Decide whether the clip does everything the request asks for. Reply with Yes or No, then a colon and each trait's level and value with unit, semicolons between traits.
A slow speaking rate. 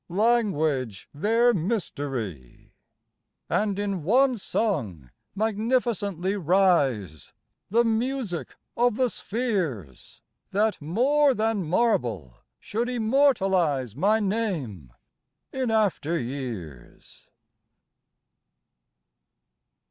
Yes: slow, 75 wpm